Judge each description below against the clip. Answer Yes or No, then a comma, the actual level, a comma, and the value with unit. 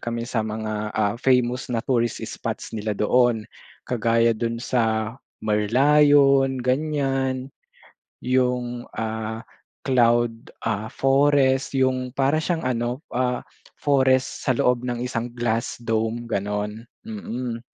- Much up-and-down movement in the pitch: No, narrow, 2.6 semitones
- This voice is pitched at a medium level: No, low, 120 Hz